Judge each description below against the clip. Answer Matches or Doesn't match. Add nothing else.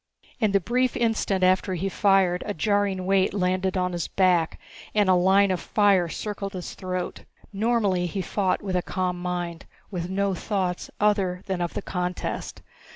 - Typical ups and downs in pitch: Doesn't match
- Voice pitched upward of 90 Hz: Matches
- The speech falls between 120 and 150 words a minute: Doesn't match